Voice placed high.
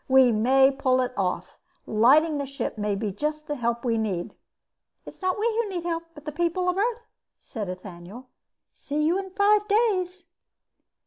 Yes: very high, 290 Hz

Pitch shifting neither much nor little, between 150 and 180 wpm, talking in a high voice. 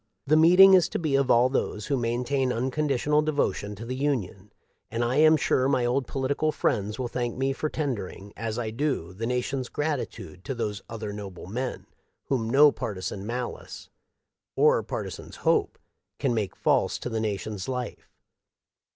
No: average, 4.3 semitones; average, 170 wpm; low, 125 Hz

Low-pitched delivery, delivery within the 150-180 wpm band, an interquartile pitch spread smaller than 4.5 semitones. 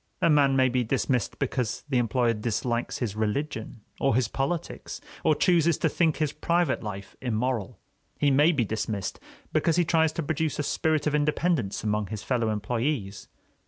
No: low, 130 Hz; average, 170 wpm; wide, 5.5 semitones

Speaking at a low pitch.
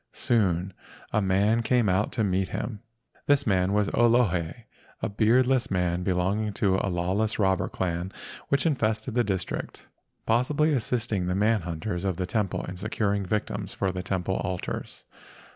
Yes: low, 100 Hz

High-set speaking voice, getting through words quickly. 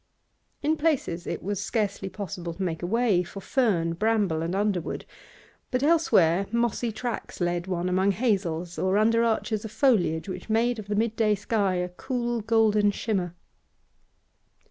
No: high, 205 Hz; average, 160 wpm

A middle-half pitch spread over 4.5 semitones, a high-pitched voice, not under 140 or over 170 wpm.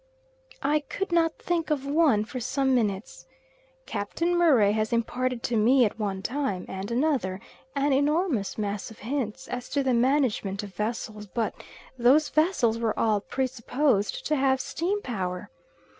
Yes: average, 5.3 semitones; very high, 250 Hz; average, 160 wpm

